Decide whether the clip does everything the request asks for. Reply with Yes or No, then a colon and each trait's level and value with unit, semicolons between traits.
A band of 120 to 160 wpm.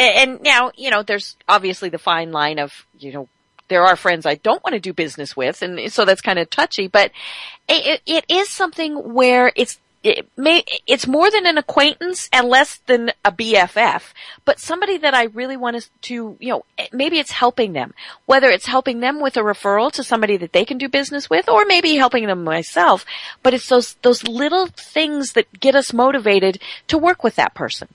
No: fast, 205 wpm